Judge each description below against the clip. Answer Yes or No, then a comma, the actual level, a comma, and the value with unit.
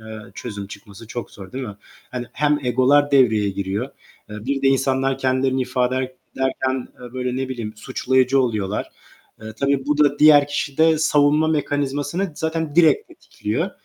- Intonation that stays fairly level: No, average, 3.0 semitones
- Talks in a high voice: No, low, 130 Hz